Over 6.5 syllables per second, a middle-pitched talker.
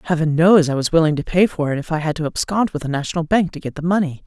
Yes: 6.9 syllables/s; medium, 165 Hz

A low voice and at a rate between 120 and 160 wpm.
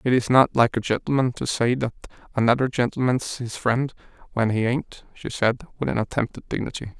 No: low, 120 Hz; average, 195 wpm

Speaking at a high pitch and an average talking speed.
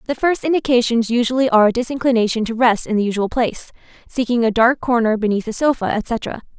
Yes: high, 235 Hz; average, 190 wpm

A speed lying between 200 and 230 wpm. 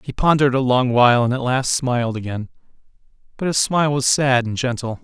Yes: fast, 205 wpm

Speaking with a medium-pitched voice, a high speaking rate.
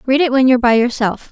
No: very high, 250 Hz; fast, 275 wpm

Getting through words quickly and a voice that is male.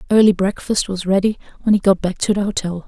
No: fast, 230 wpm; female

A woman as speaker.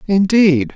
No: male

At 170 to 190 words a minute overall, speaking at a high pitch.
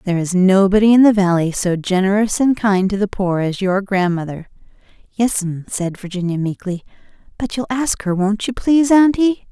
Yes: average, 175 wpm; high, 200 Hz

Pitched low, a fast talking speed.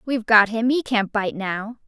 No: high, 220 Hz; fast, 225 wpm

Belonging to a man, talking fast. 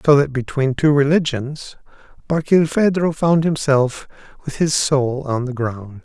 No: male; average, 140 wpm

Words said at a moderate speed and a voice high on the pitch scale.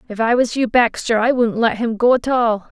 No: fast, 260 wpm; high, 235 Hz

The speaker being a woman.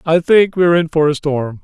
No: male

